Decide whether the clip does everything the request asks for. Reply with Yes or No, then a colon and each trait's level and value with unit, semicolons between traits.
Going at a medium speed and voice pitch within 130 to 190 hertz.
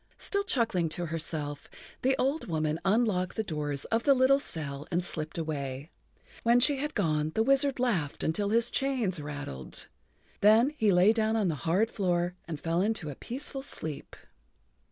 Yes: average, 170 wpm; medium, 185 Hz